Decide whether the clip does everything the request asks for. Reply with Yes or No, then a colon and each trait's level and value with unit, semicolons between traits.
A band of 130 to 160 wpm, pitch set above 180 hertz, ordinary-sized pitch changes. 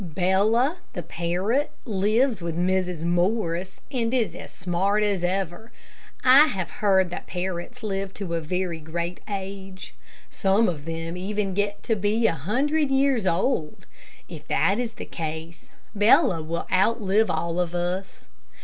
Yes: average, 150 wpm; high, 190 Hz; average, 3.9 semitones